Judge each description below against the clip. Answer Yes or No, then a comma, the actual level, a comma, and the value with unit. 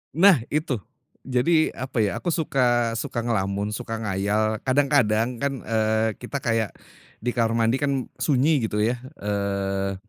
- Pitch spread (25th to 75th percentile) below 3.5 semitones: No, average, 4.0 semitones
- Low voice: Yes, low, 115 Hz